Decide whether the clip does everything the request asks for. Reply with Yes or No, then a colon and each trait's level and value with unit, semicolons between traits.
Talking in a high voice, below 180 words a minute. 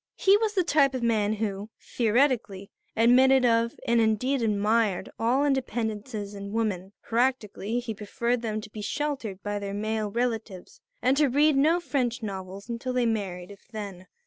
Yes: high, 225 Hz; average, 170 wpm